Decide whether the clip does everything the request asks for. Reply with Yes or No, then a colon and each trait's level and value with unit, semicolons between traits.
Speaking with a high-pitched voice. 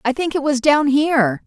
Yes: very high, 275 Hz